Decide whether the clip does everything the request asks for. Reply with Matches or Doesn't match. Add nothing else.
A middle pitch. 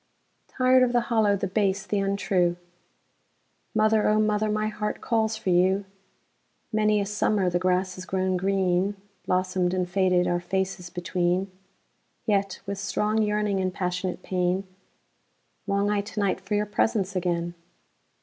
Doesn't match